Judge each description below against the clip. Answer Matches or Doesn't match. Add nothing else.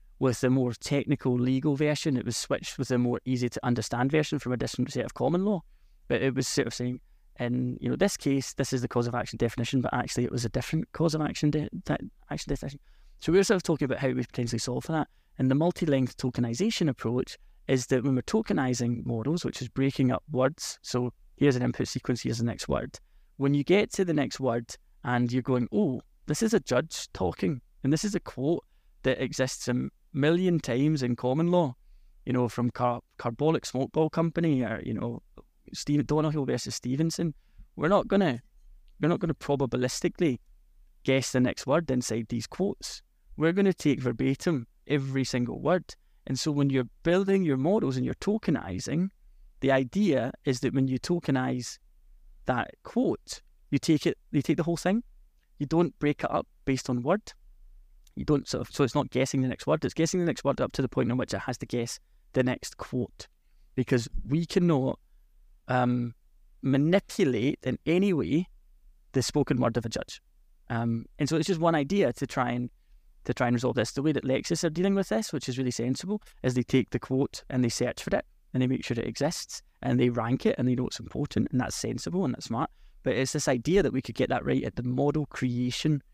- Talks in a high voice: Doesn't match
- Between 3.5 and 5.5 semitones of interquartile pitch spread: Matches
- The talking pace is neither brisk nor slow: Doesn't match